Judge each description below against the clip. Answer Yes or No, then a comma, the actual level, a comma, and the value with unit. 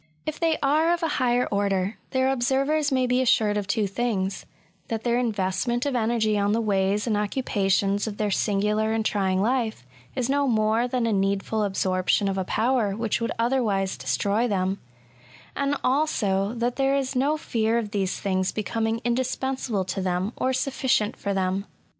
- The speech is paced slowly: No, average, 175 wpm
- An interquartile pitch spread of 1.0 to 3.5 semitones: No, average, 4.3 semitones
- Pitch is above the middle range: Yes, high, 220 Hz